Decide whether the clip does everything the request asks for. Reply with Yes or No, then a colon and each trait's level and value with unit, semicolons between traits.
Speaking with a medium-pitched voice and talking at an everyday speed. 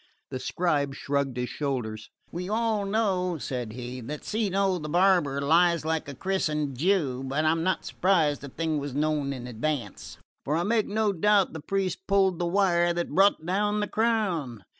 Yes: medium, 165 Hz; average, 180 wpm